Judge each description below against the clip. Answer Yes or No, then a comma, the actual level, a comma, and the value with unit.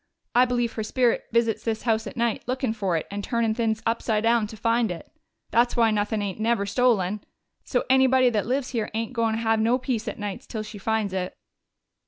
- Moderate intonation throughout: No, narrow, 2.0 semitones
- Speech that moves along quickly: Yes, fast, 210 wpm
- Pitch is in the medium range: No, high, 225 Hz